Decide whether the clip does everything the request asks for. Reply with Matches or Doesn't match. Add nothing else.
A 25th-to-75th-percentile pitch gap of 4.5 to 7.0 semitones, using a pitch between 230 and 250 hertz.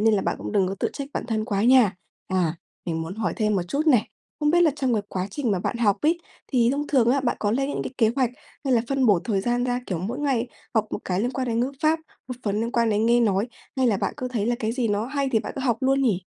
Doesn't match